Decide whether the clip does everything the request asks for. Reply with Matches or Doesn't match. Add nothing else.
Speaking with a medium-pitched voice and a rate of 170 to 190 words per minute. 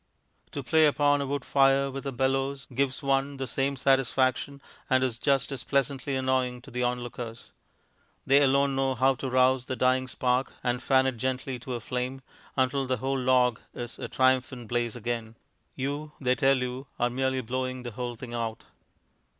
Doesn't match